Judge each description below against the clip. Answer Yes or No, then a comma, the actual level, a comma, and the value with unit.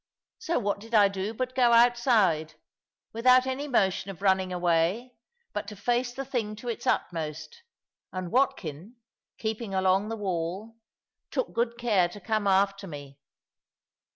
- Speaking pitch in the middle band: No, high, 205 Hz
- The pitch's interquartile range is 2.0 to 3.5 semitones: No, average, 4.4 semitones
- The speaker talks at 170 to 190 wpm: No, average, 150 wpm